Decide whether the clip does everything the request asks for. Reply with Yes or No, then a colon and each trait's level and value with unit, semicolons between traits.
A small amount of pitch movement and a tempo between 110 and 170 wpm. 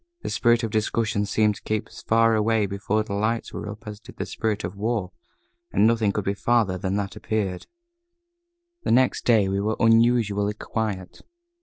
No: narrow, 2.1 semitones; average, 185 wpm